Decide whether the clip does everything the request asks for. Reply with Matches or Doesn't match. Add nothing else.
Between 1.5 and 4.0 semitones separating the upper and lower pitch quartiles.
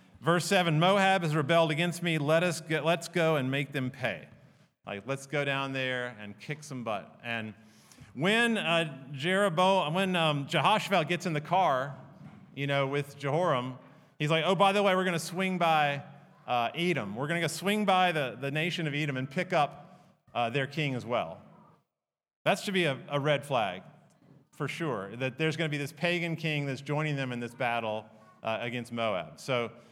Doesn't match